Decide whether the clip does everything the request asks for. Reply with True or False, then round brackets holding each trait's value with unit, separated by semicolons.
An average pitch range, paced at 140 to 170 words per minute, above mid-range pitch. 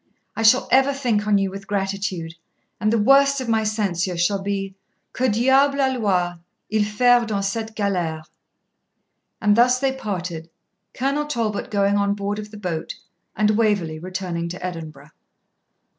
True (3.9 semitones; 155 wpm; 205 Hz)